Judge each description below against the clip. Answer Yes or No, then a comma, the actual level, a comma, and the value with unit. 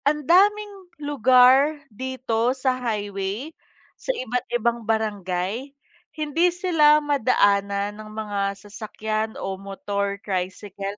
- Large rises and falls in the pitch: Yes, wide, 6.0 semitones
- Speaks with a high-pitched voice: Yes, high, 225 Hz